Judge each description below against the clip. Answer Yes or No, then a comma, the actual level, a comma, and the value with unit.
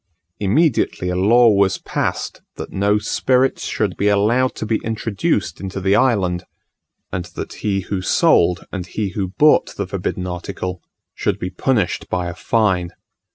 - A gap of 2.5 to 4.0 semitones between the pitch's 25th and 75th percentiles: Yes, average, 3.1 semitones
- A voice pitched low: Yes, low, 100 Hz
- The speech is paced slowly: No, average, 155 wpm